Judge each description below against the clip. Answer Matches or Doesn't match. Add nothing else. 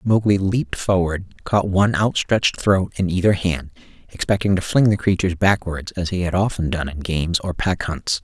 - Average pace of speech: Matches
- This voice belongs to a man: Matches